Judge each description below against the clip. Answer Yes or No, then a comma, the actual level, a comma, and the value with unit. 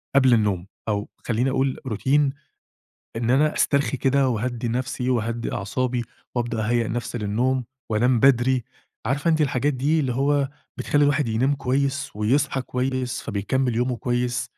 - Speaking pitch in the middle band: No, low, 125 Hz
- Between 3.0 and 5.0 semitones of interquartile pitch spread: No, narrow, 2.6 semitones